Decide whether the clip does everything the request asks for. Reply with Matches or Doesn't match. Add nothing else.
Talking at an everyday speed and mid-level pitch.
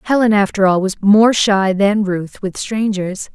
Doesn't match